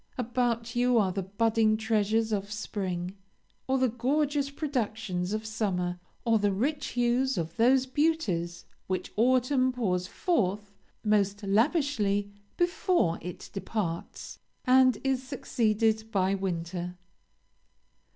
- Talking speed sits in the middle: No, slow, 115 wpm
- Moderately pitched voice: No, high, 220 Hz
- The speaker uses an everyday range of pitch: Yes, average, 4.6 semitones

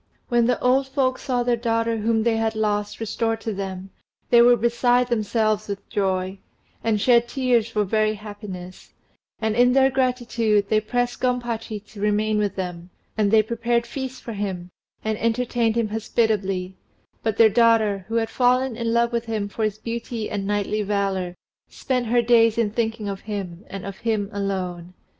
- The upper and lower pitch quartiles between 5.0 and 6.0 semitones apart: No, narrow, 2.6 semitones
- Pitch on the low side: No, high, 220 Hz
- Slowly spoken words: No, average, 175 wpm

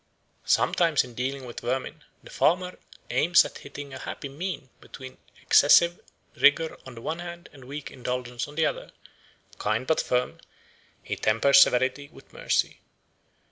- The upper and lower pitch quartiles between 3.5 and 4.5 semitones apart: Yes, average, 4.1 semitones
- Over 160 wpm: No, average, 150 wpm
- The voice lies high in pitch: No, medium, 140 Hz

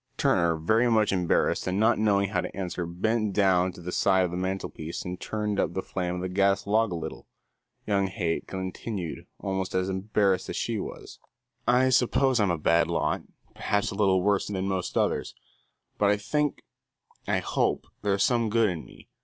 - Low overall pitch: Yes, very low, 95 Hz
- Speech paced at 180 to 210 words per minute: Yes, average, 185 wpm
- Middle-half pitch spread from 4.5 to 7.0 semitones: No, average, 2.7 semitones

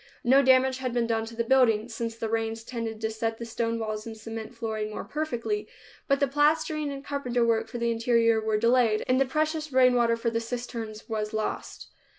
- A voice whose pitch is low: No, high, 230 Hz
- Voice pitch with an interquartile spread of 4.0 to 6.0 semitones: No, narrow, 2.5 semitones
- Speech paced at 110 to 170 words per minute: No, fast, 205 wpm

